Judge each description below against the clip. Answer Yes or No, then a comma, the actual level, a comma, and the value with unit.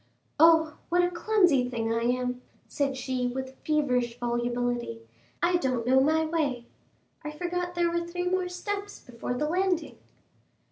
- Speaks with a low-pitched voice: No, very high, 290 Hz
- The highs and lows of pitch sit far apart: Yes, wide, 6.0 semitones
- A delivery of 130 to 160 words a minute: Yes, average, 150 wpm